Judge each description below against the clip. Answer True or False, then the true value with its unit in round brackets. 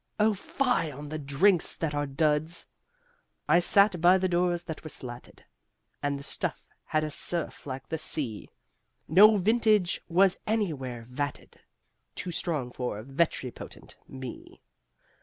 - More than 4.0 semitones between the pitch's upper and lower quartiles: True (4.9 semitones)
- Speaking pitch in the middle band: True (160 Hz)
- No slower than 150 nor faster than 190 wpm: False (140 wpm)